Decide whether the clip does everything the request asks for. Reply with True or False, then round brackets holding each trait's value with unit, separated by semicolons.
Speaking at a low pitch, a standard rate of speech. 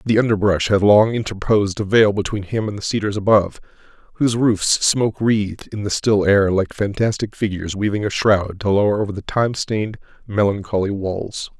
True (105 Hz; 180 wpm)